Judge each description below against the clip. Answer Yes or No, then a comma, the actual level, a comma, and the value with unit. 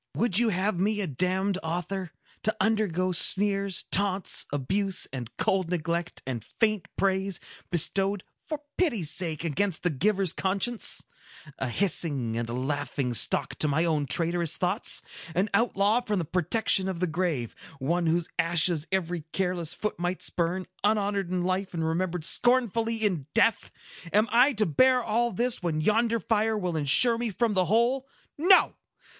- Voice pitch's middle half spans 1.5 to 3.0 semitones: No, average, 4.2 semitones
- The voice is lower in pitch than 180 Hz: No, medium, 185 Hz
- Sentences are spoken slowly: No, average, 155 wpm